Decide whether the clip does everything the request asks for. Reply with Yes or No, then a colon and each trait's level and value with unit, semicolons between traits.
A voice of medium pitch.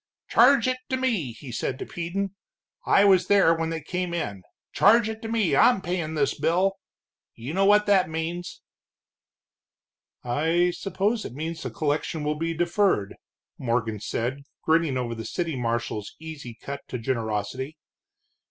Yes: medium, 165 Hz